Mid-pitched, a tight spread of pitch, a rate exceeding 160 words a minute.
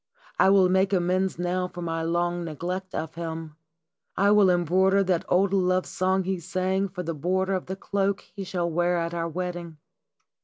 Yes: medium, 180 Hz; narrow, 1.7 semitones; average, 185 wpm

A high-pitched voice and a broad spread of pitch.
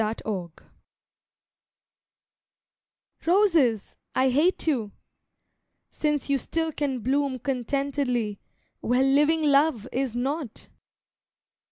No: very high, 270 Hz; average, 3.7 semitones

